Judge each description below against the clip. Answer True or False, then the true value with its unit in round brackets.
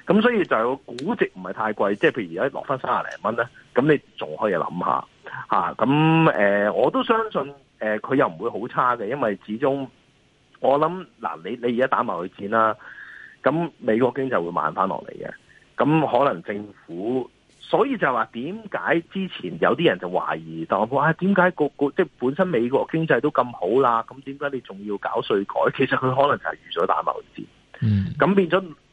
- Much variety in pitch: True (7.1 semitones)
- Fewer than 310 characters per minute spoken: True (280 characters per minute)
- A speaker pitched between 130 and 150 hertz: True (135 Hz)